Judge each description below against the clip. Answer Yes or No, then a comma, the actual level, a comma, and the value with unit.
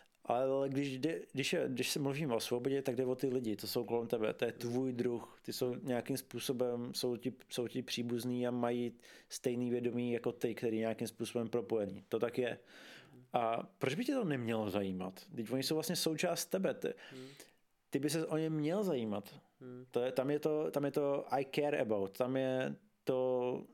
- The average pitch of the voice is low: Yes, low, 125 Hz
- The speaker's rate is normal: No, fast, 200 wpm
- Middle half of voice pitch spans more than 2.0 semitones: Yes, narrow, 2.4 semitones